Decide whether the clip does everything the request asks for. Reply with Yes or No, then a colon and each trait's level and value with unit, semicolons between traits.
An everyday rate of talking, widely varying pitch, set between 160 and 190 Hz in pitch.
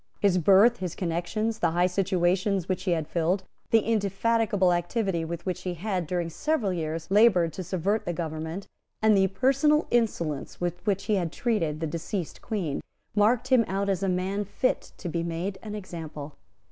No: average, 180 wpm; average, 3.6 semitones; medium, 185 Hz